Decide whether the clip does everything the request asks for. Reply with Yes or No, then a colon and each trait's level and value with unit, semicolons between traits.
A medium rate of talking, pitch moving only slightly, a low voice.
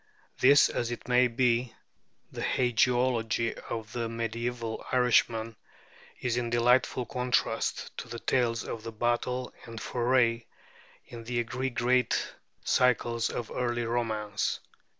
No: slow, 120 wpm; narrow, 1.3 semitones; low, 120 Hz